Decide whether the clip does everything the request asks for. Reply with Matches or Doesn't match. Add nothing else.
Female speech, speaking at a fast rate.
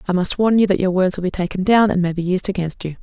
Matches